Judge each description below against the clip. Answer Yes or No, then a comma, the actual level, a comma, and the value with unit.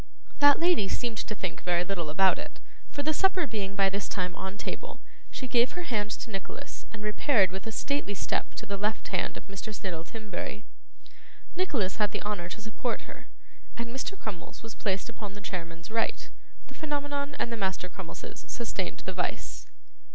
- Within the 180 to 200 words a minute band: Yes, average, 190 wpm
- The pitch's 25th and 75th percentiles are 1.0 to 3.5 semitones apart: No, average, 4.3 semitones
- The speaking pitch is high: Yes, high, 210 Hz